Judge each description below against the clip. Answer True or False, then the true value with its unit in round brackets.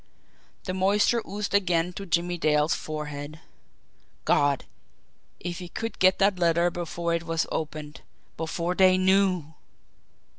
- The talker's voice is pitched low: False (175 Hz)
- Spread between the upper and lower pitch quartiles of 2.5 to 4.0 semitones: True (2.9 semitones)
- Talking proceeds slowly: True (125 wpm)